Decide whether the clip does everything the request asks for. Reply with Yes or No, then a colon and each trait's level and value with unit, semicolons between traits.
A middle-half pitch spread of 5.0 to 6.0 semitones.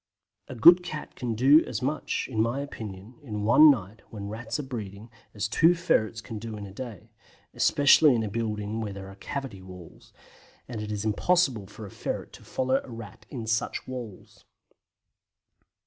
No: average, 4.0 semitones